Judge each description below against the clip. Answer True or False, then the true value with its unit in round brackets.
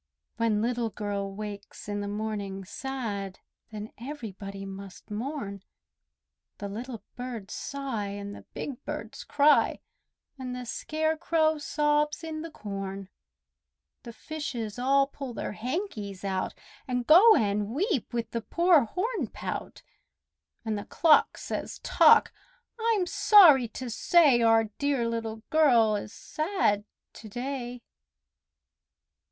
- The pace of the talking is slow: True (125 wpm)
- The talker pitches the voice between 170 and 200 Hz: False (235 Hz)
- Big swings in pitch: True (6.2 semitones)